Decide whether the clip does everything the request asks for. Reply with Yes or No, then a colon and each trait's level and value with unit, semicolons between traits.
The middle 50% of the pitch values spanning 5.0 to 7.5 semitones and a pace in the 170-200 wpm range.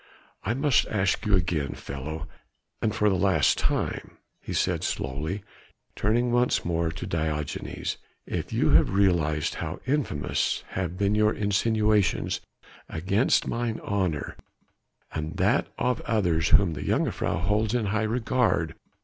No: average, 5.3 semitones; slow, 135 wpm